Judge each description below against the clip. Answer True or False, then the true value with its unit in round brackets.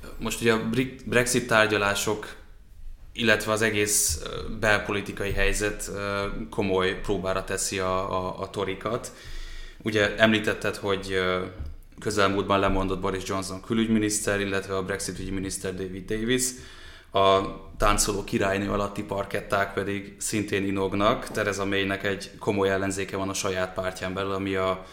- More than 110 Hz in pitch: False (100 Hz)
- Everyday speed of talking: True (125 wpm)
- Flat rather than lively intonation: True (1.6 semitones)